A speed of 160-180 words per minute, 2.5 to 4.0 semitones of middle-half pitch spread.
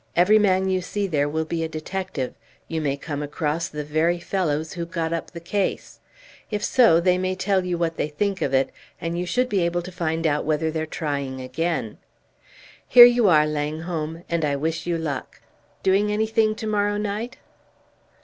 No: average, 190 wpm; average, 3.7 semitones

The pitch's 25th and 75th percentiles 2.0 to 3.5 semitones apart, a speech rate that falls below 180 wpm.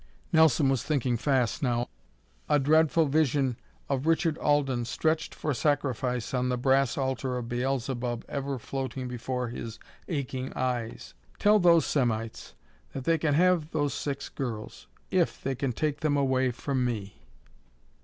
Yes: average, 2.9 semitones; average, 145 wpm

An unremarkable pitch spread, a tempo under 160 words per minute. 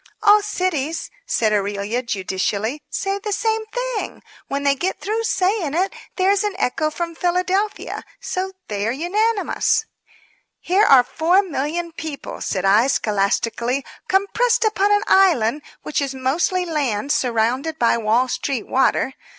No: wide, 7.9 semitones; average, 140 wpm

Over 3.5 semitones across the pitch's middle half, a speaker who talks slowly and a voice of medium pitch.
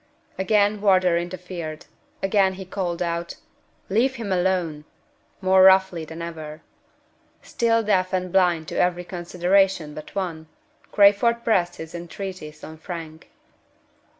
No: narrow, 2.4 semitones; slow, 125 wpm; medium, 180 Hz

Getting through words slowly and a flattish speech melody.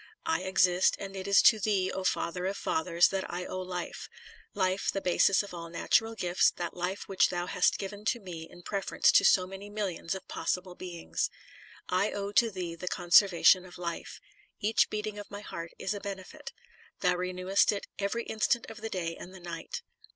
No: average, 200 wpm; narrow, 2.2 semitones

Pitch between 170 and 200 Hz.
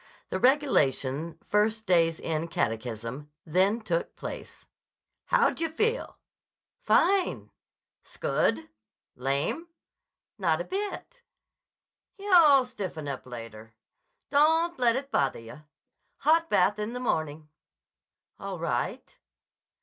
Yes: medium, 185 Hz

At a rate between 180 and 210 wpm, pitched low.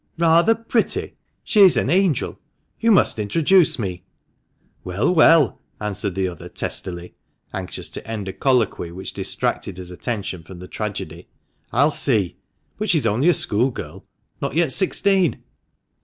No: average, 155 wpm; low, 115 Hz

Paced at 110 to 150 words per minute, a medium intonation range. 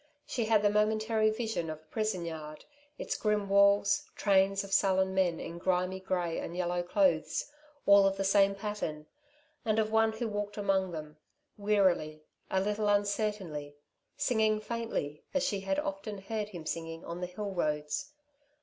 No: average, 165 wpm; average, 3.3 semitones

